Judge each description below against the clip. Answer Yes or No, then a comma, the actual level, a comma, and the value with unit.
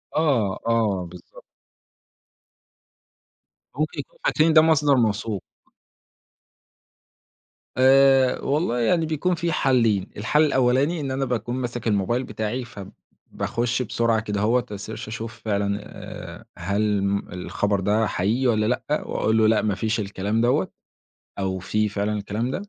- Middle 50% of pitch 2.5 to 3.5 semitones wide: No, average, 4.2 semitones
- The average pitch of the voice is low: Yes, low, 115 Hz